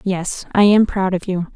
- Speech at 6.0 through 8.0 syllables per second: No, 4.6 syllables/s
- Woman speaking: Yes, female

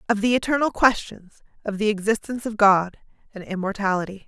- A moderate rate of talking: Yes, average, 155 wpm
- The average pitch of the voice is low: No, high, 210 Hz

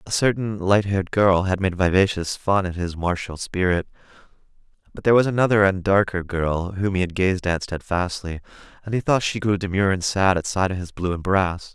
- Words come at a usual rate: No, fast, 210 wpm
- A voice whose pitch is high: No, very low, 95 Hz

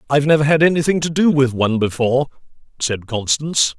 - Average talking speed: Yes, average, 175 wpm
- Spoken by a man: Yes, male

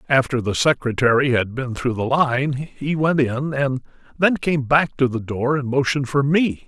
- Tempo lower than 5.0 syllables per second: Yes, 4.6 syllables/s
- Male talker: Yes, male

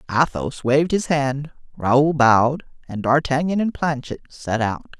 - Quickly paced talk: No, average, 145 wpm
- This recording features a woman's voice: No, male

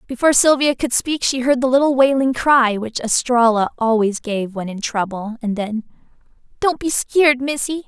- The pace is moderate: Yes, average, 175 wpm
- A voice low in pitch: No, very high, 250 Hz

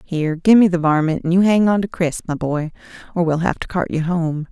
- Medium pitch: Yes, medium, 170 Hz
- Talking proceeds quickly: Yes, fast, 265 wpm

